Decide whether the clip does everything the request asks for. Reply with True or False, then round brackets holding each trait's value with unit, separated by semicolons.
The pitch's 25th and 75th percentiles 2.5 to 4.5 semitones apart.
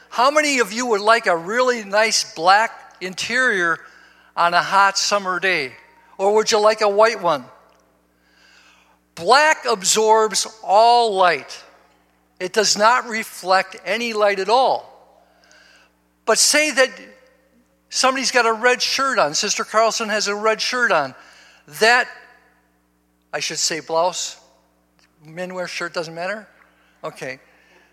False (5.3 semitones)